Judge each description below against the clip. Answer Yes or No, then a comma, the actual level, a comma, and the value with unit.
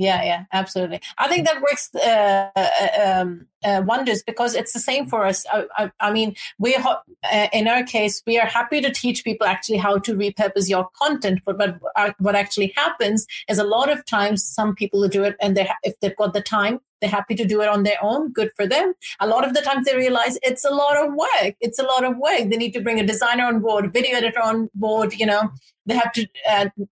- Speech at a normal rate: No, fast, 245 wpm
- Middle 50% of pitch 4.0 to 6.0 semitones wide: No, average, 3.2 semitones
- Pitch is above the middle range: Yes, high, 220 Hz